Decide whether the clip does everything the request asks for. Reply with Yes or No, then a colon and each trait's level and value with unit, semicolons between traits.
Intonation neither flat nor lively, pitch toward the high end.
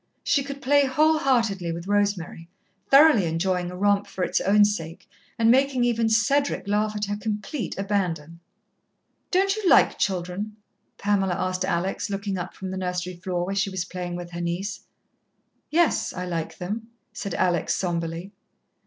Yes: average, 3.9 semitones; high, 195 Hz